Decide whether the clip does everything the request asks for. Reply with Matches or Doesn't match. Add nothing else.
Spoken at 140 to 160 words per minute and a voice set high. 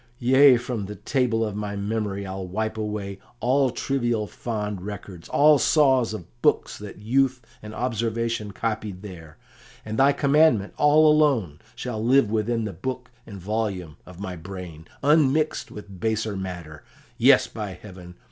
Doesn't match